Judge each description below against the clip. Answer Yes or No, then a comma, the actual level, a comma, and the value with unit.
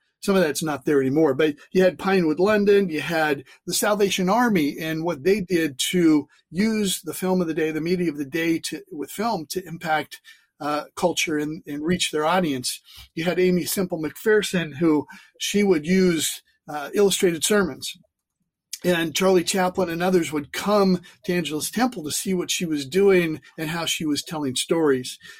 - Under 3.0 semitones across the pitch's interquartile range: No, average, 3.6 semitones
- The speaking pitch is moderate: Yes, medium, 175 Hz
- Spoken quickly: No, average, 185 wpm